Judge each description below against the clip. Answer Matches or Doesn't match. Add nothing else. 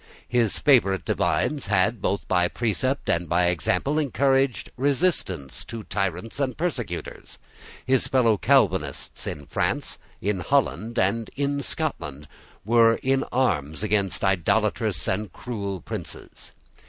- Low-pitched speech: Matches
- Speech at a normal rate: Doesn't match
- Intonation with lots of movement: Matches